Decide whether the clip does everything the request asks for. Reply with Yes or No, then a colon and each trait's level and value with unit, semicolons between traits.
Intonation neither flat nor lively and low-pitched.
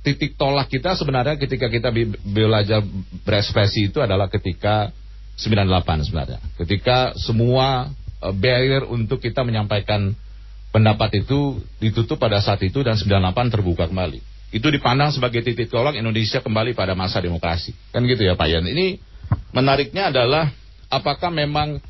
Yes: average, 4.9 semitones; low, 110 Hz